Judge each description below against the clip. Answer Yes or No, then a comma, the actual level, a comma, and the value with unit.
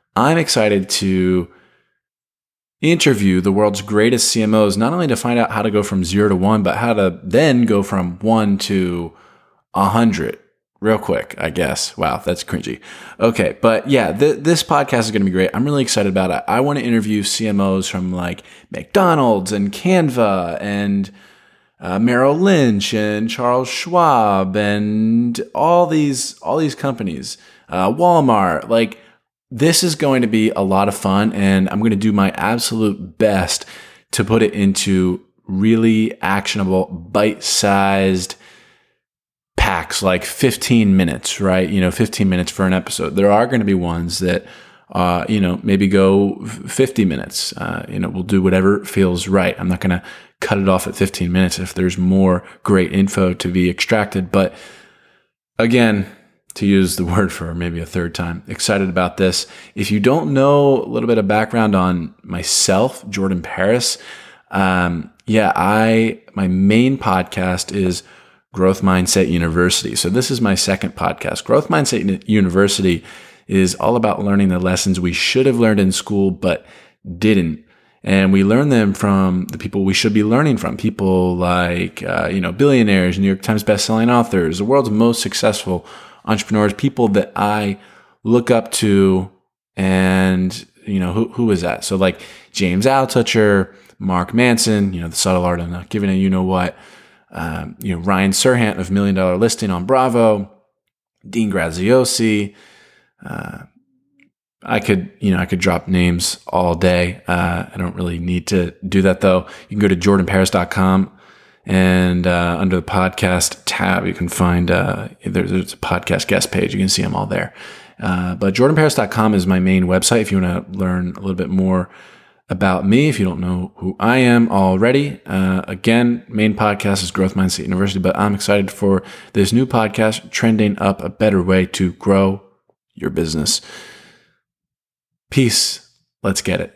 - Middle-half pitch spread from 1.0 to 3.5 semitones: Yes, average, 3.2 semitones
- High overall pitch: No, low, 100 Hz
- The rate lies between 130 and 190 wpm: Yes, average, 170 wpm